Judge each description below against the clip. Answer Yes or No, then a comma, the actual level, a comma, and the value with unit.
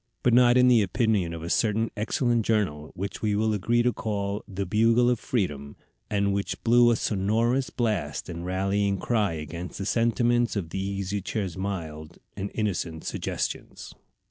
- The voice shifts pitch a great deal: No, average, 3.7 semitones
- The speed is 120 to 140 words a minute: No, average, 170 wpm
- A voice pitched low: Yes, low, 100 Hz